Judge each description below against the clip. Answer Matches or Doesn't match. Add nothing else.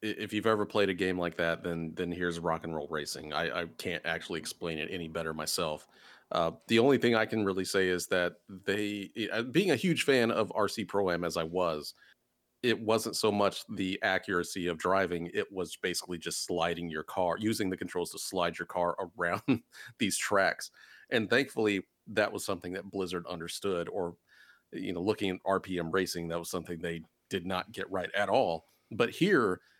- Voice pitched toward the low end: Matches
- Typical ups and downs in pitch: Matches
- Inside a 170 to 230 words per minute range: Matches